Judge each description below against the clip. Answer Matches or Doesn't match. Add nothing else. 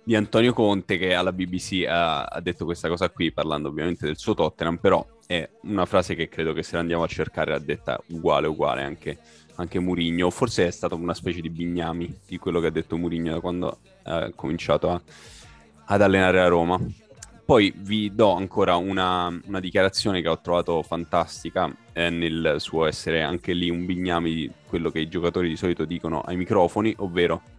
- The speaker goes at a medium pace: Doesn't match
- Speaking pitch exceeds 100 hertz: Doesn't match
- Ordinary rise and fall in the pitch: Doesn't match